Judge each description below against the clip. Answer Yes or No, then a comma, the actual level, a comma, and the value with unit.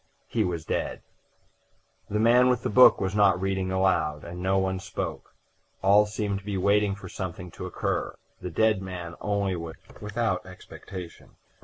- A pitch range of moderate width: No, narrow, 2.2 semitones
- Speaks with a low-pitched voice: Yes, very low, 95 Hz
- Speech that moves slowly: No, average, 165 wpm